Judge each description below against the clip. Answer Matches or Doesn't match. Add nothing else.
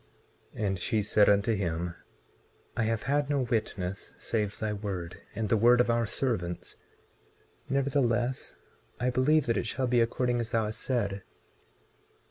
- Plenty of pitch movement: Doesn't match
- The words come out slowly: Doesn't match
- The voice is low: Matches